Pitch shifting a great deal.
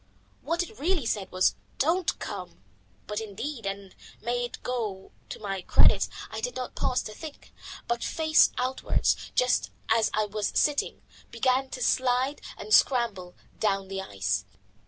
No: average, 4.9 semitones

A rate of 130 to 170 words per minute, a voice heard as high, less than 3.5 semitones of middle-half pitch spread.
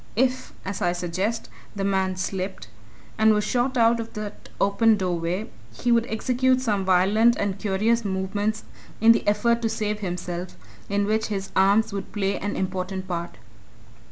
Yes: average, 160 wpm; high, 205 Hz; average, 2.9 semitones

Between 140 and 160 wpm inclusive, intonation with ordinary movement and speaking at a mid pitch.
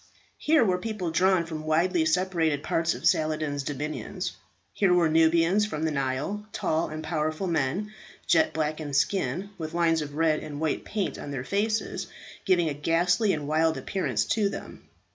No: average, 170 wpm; average, 3.4 semitones; medium, 165 Hz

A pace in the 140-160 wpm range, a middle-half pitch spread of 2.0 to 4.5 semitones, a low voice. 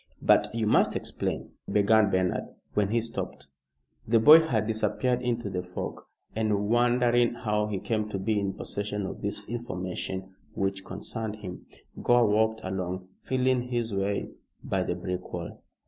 Yes: average, 155 wpm; average, 3.4 semitones; low, 105 Hz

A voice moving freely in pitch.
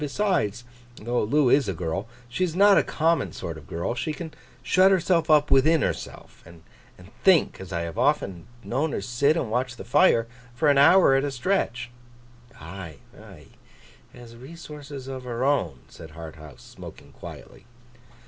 Yes: wide, 7.5 semitones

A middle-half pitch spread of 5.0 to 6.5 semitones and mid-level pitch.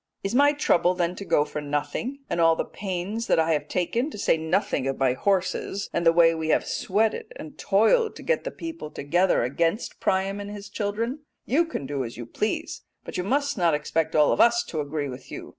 Yes: wide, 5.6 semitones; medium, 180 Hz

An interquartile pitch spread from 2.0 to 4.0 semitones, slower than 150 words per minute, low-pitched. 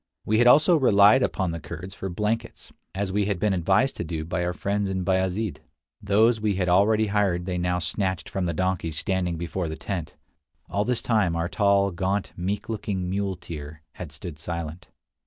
No: average, 2.8 semitones; average, 190 wpm; very low, 95 Hz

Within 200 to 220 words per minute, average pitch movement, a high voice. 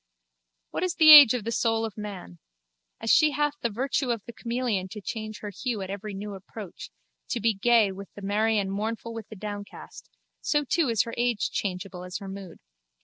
Yes: fast, 205 wpm; average, 3.1 semitones; high, 215 Hz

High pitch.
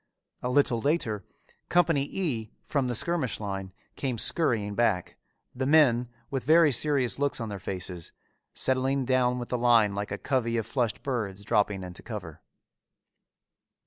No: low, 125 Hz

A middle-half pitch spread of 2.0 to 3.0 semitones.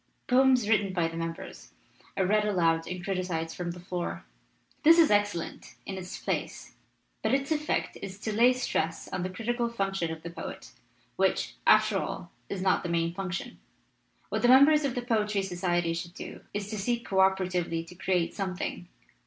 No: average, 3.9 semitones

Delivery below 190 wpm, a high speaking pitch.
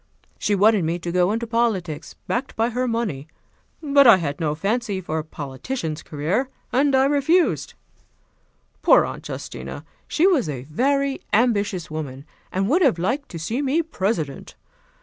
Yes: average, 160 wpm; high, 210 Hz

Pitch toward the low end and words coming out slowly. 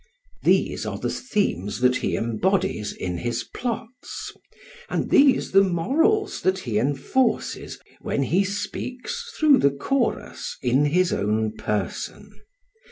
No: medium, 180 Hz; slow, 125 wpm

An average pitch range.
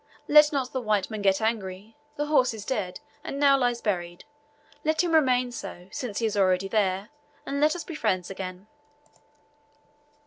No: wide, 6.1 semitones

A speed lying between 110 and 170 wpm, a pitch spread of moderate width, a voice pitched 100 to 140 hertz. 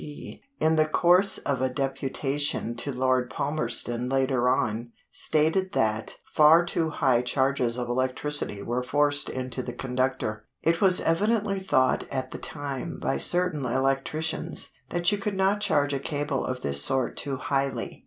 Yes: average, 155 wpm; average, 3.9 semitones; low, 135 Hz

